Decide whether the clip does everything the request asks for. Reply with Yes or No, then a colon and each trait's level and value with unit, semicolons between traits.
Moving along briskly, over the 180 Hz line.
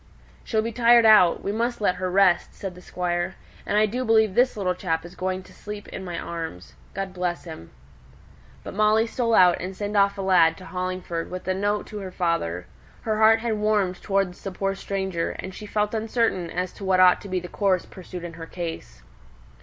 Yes: fast, 215 wpm; high, 190 Hz